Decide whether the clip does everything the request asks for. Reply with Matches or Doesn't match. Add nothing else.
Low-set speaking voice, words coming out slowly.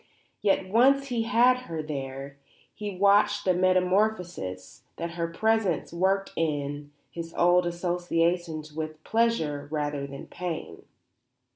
Doesn't match